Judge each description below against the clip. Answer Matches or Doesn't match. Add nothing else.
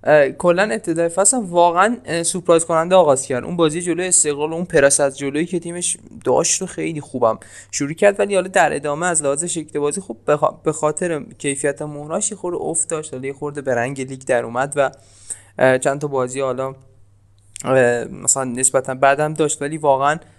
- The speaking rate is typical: Doesn't match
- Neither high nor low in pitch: Matches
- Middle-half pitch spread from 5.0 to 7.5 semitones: Doesn't match